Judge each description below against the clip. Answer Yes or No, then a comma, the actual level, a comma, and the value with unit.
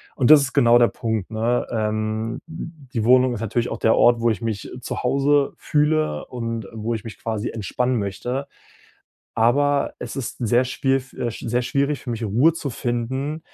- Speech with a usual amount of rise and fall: Yes, average, 3.4 semitones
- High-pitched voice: No, low, 120 Hz